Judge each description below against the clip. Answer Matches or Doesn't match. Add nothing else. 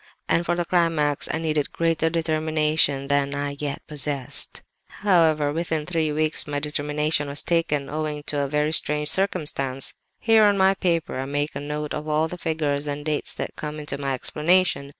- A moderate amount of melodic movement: Doesn't match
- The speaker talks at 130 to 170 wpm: Doesn't match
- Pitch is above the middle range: Doesn't match